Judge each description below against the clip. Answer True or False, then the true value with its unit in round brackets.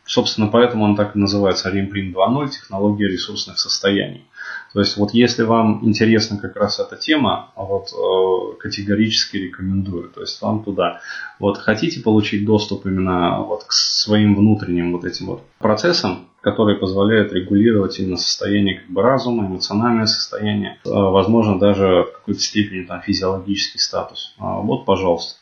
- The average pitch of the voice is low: True (100 Hz)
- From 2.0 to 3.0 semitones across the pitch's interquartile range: True (2.5 semitones)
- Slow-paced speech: False (145 wpm)